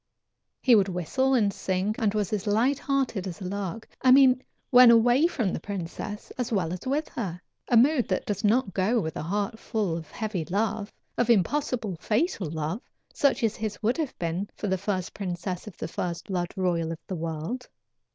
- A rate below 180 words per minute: No, average, 200 wpm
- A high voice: Yes, high, 205 Hz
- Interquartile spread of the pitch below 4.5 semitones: No, average, 4.9 semitones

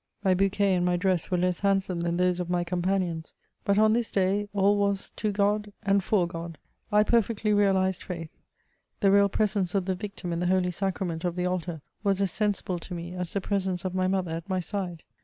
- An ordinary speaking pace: No, fast, 215 wpm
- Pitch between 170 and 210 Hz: Yes, medium, 185 Hz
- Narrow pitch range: Yes, narrow, 2.1 semitones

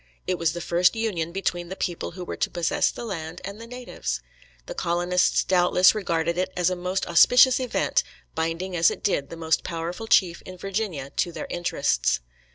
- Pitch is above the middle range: No, medium, 175 Hz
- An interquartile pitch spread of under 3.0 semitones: Yes, narrow, 2.4 semitones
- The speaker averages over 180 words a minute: Yes, average, 190 wpm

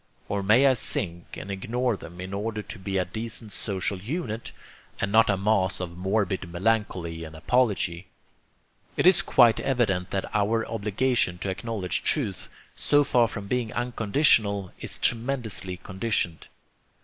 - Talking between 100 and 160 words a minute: Yes, average, 150 wpm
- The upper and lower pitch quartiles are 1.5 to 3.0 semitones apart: No, average, 3.7 semitones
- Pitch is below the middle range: Yes, low, 105 Hz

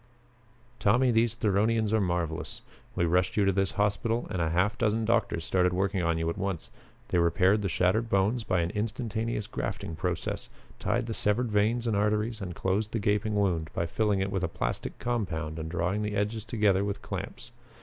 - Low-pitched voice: Yes, low, 100 Hz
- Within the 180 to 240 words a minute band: Yes, average, 190 wpm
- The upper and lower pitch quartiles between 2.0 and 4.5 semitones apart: Yes, average, 3.3 semitones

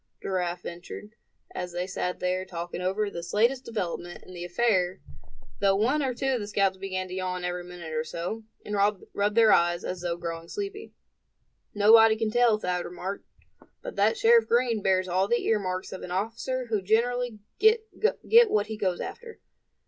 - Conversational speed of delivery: Yes, average, 180 wpm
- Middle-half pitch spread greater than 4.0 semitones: Yes, average, 4.5 semitones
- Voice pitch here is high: Yes, high, 195 Hz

